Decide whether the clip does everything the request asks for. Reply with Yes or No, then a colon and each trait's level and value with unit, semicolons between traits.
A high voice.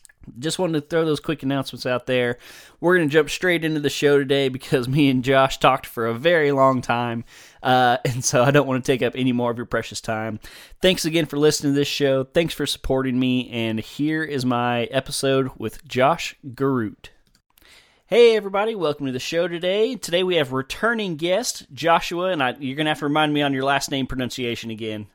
No: low, 135 Hz